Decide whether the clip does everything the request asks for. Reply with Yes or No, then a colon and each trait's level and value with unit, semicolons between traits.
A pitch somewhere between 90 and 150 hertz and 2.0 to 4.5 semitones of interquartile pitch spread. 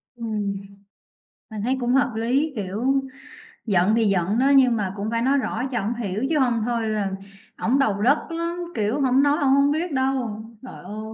No: high, 235 Hz; average, 4.0 semitones